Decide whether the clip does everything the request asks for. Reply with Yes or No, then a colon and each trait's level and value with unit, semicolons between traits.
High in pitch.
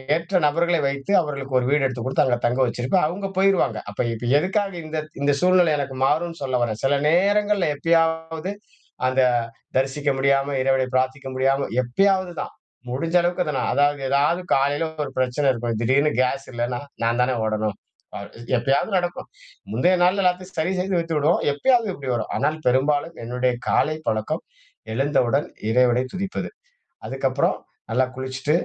No: medium, 140 Hz